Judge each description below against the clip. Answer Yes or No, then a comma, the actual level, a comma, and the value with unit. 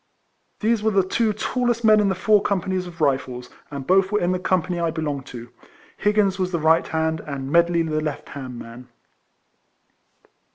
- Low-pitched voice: No, medium, 175 Hz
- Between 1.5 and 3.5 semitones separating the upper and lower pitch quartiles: No, average, 5.2 semitones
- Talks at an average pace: Yes, average, 180 wpm